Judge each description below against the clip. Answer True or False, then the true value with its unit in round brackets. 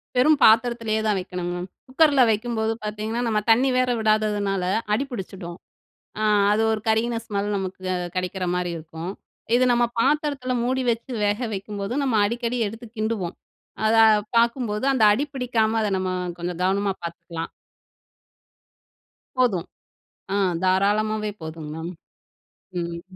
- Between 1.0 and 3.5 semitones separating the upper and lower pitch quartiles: False (4.1 semitones)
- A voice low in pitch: False (215 Hz)